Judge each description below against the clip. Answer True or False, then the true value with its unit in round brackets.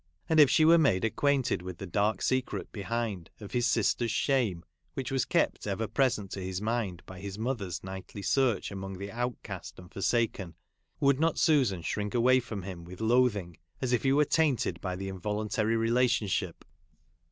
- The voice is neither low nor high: False (110 Hz)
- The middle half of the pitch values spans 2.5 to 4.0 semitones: False (4.8 semitones)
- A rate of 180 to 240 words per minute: True (185 wpm)